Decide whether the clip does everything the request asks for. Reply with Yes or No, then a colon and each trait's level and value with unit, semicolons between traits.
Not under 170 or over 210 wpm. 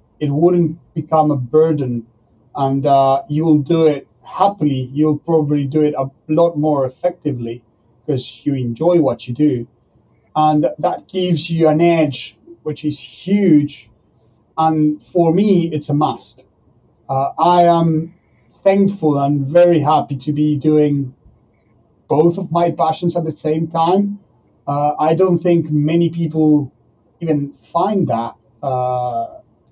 No: average, 140 wpm